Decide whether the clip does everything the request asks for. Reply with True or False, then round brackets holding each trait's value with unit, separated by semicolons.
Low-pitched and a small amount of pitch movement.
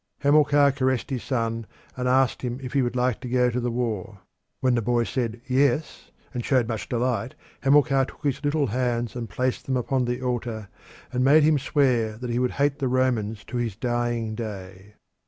True (125 Hz; 2.3 semitones)